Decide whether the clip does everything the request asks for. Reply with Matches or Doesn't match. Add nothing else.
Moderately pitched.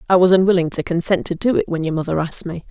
Matches